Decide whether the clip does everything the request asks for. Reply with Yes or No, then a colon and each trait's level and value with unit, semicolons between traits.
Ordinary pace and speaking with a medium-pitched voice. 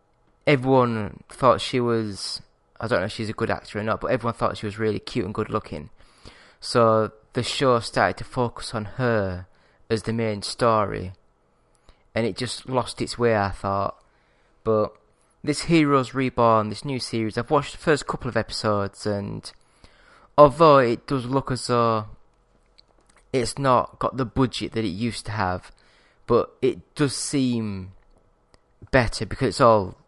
No: average, 165 wpm; low, 115 Hz